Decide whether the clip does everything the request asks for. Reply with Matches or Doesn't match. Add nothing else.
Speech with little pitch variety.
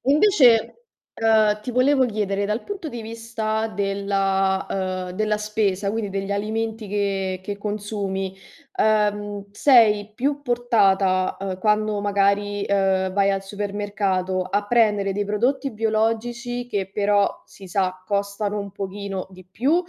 Matches